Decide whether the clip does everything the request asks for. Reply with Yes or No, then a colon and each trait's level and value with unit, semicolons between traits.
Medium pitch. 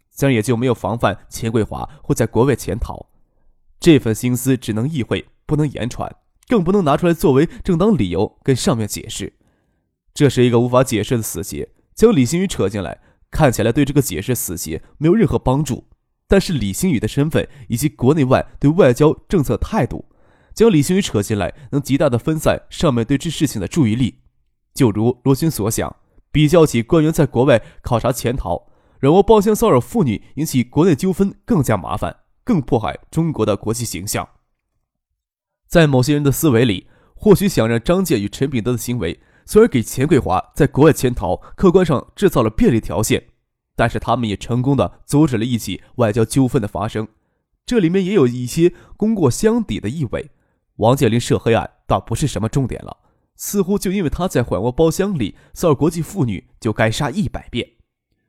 No: low, 125 Hz